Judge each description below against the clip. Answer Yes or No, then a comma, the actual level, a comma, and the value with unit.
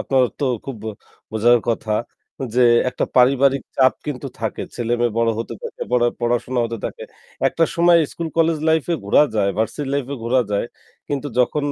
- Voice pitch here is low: Yes, low, 125 Hz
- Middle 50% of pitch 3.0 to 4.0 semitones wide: Yes, average, 3.4 semitones